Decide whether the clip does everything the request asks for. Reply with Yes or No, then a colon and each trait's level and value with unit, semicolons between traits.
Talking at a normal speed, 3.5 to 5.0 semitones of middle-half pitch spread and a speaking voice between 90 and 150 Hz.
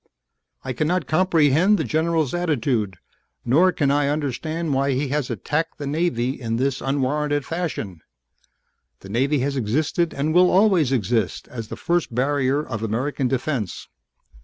Yes: average, 145 wpm; average, 4.0 semitones; medium, 140 Hz